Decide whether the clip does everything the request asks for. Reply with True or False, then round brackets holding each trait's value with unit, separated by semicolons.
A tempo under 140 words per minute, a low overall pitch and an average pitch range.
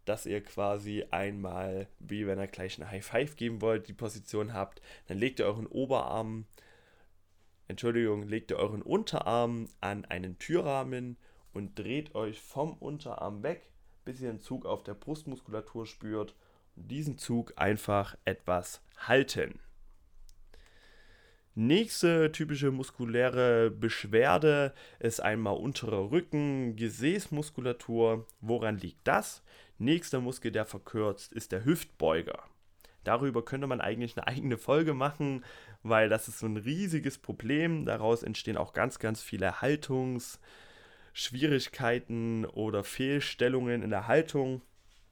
True (125 wpm; 115 Hz; 4.5 semitones)